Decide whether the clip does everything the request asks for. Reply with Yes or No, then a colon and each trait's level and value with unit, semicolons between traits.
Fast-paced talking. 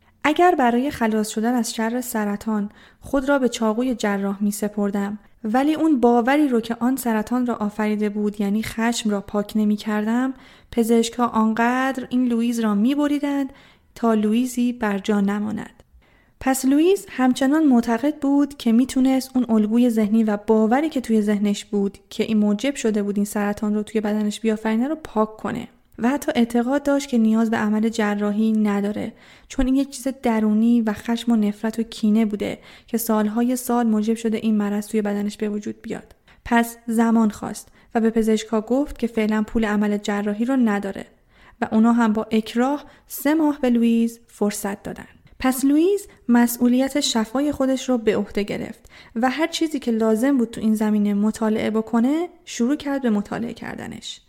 Yes: fast, 175 wpm